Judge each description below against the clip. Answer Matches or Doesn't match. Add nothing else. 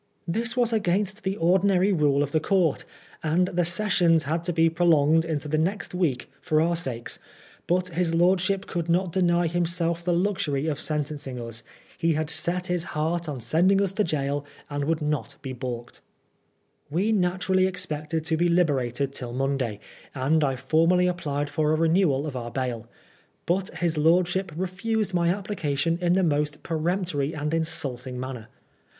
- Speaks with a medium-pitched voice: Matches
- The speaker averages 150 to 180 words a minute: Matches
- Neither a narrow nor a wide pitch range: Matches